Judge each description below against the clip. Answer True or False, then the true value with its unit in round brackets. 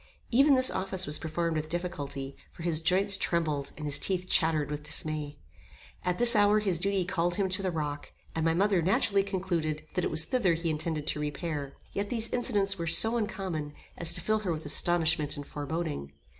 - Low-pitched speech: False (170 Hz)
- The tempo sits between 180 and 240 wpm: True (200 wpm)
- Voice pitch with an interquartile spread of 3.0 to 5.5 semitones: True (4.1 semitones)